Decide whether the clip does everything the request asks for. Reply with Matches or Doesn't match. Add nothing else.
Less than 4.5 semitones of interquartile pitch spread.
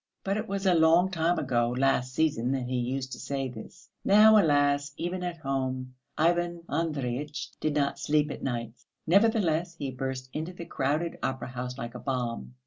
Doesn't match